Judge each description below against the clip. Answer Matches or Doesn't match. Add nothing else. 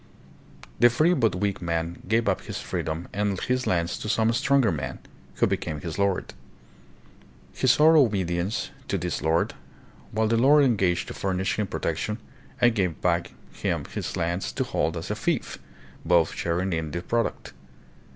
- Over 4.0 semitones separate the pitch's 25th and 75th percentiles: Matches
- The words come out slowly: Doesn't match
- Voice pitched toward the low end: Matches